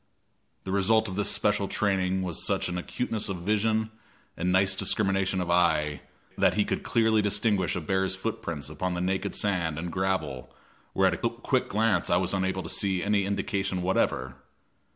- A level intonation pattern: Yes, narrow, 2.3 semitones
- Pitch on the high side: No, very low, 95 Hz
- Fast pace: No, average, 175 wpm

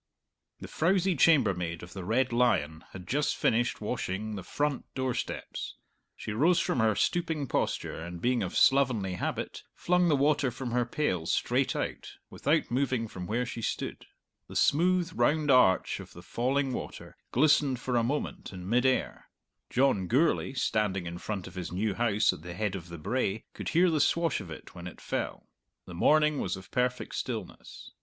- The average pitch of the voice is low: Yes, low, 120 Hz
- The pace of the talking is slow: No, average, 180 wpm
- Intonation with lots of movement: Yes, wide, 6.8 semitones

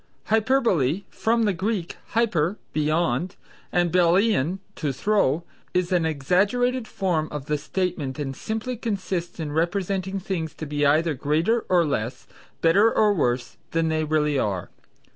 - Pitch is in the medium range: Yes, medium, 175 Hz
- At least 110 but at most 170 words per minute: Yes, average, 140 wpm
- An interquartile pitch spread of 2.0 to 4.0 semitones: No, average, 5.0 semitones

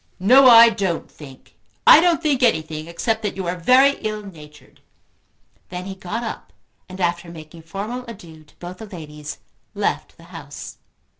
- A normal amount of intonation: No, wide, 6.1 semitones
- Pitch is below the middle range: No, medium, 185 Hz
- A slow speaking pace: No, average, 165 wpm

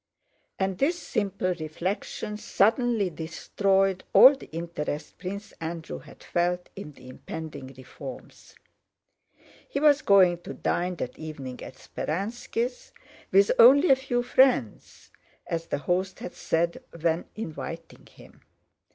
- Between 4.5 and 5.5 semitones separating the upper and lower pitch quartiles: Yes, average, 5.0 semitones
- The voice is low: No, medium, 180 Hz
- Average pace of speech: No, slow, 125 wpm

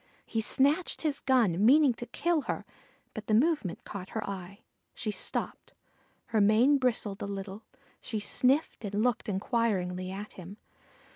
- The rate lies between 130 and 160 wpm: Yes, average, 150 wpm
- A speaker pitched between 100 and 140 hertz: No, high, 220 Hz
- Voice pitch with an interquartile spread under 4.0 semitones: No, average, 4.4 semitones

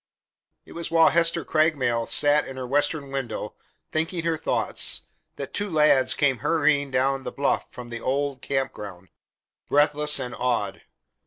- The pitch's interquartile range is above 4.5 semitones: No, average, 3.3 semitones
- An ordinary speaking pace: Yes, average, 155 wpm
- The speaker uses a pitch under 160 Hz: Yes, medium, 140 Hz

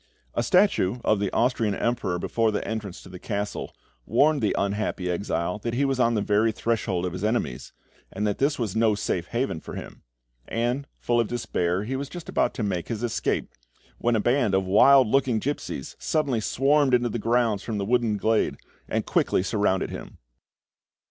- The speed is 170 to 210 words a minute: Yes, average, 190 wpm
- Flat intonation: No, average, 3.4 semitones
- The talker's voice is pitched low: Yes, low, 110 Hz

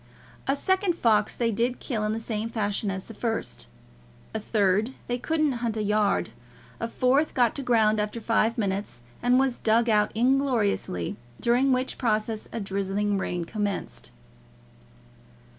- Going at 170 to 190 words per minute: No, average, 155 wpm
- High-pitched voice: Yes, high, 225 Hz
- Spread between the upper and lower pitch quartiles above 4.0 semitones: No, average, 2.9 semitones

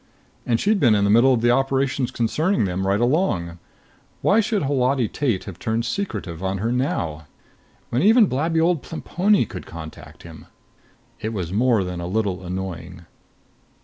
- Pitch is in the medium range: No, low, 115 Hz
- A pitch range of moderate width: No, wide, 6.8 semitones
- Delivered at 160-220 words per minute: Yes, average, 165 wpm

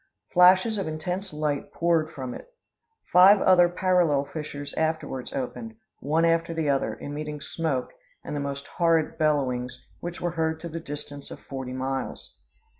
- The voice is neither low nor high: Yes, medium, 155 Hz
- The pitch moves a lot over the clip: No, average, 3.4 semitones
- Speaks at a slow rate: No, average, 155 wpm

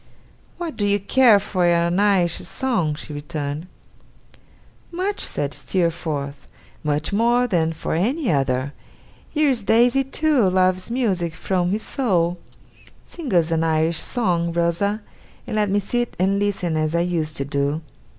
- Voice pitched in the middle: Yes, medium, 180 Hz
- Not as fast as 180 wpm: Yes, average, 150 wpm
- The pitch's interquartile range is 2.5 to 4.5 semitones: No, wide, 5.4 semitones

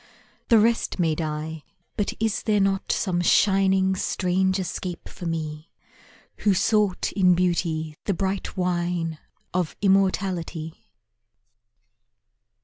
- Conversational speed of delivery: No, slow, 110 wpm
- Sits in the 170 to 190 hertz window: Yes, medium, 185 Hz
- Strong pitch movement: No, average, 2.8 semitones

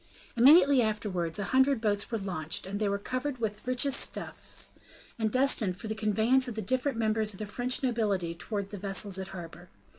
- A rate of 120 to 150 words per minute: No, average, 190 wpm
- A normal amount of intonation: Yes, average, 4.2 semitones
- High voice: Yes, high, 215 Hz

